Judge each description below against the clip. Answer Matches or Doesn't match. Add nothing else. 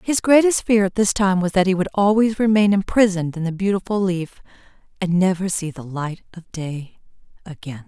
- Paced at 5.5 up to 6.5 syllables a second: Doesn't match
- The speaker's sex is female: Matches